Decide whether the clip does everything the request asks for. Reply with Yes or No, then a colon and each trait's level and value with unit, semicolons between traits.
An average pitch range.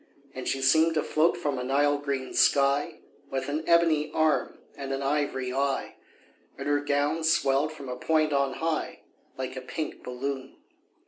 No: narrow, 2.3 semitones